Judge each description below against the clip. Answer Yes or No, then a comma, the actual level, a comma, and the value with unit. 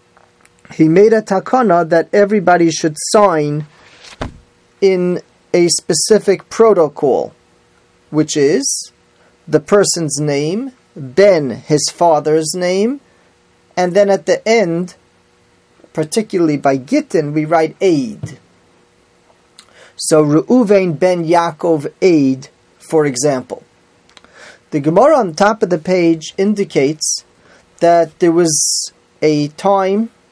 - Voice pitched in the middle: Yes, medium, 170 Hz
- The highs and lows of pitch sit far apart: No, average, 4.6 semitones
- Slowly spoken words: Yes, slow, 105 wpm